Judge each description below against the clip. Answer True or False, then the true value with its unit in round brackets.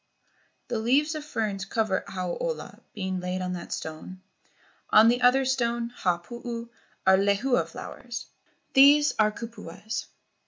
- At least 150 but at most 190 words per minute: False (135 wpm)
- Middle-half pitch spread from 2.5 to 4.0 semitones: False (4.6 semitones)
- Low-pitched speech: False (225 Hz)